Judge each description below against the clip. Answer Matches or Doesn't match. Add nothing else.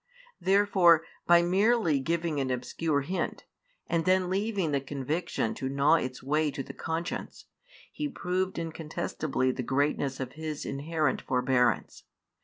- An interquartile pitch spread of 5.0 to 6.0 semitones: Doesn't match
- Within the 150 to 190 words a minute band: Doesn't match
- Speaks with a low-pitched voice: Doesn't match